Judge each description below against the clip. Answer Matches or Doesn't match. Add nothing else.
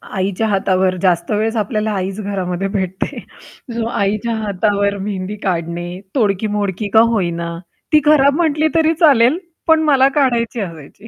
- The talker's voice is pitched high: Matches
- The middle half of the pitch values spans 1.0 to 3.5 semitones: Doesn't match